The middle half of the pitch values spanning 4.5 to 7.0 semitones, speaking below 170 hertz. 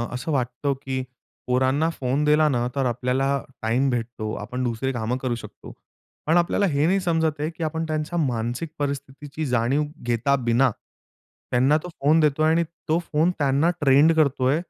No: average, 3.8 semitones; medium, 140 Hz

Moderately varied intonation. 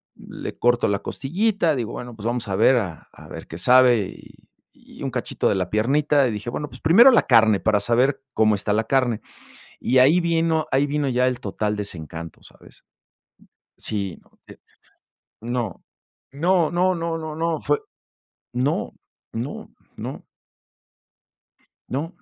No: wide, 6.0 semitones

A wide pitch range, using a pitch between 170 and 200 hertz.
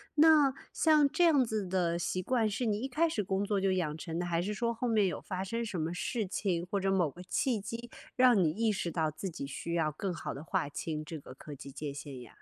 Yes: wide, 5.8 semitones; high, 190 Hz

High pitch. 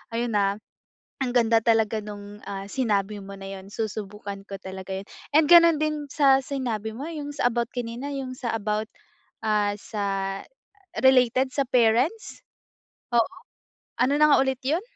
Yes: high, 230 Hz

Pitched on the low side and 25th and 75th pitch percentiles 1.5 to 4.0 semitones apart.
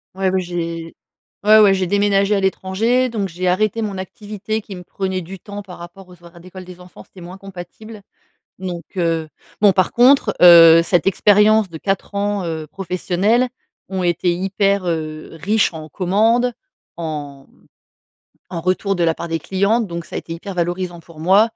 No: medium, 185 Hz; average, 2.9 semitones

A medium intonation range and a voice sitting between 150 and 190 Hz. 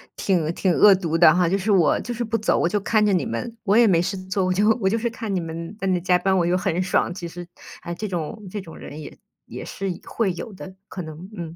Yes: average, 3.3 semitones; medium, 185 Hz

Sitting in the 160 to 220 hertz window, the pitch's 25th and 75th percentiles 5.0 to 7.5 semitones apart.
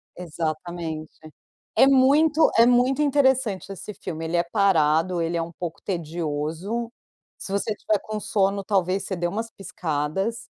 Yes: high, 190 Hz; average, 5.3 semitones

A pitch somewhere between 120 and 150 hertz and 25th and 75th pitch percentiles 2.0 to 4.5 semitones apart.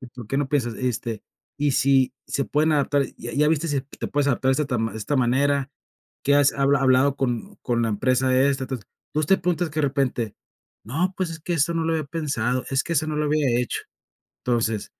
Yes: medium, 140 Hz; average, 3.1 semitones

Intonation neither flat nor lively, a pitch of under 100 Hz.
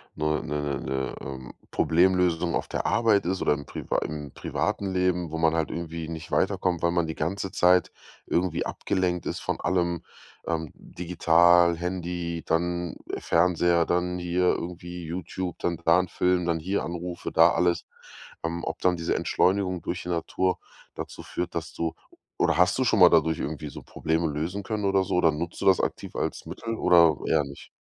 No: narrow, 1.8 semitones; very low, 85 Hz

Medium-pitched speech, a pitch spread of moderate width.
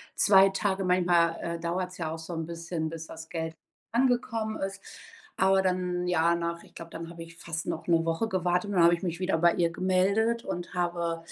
No: medium, 175 Hz; narrow, 2.1 semitones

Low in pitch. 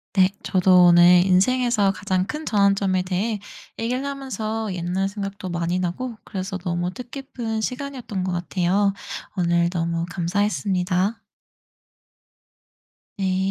No: high, 190 Hz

